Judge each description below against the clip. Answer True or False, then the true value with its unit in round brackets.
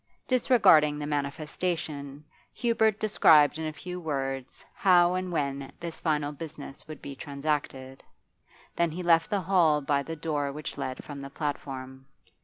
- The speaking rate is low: False (150 wpm)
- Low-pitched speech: False (150 Hz)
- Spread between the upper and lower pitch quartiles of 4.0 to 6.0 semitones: False (3.5 semitones)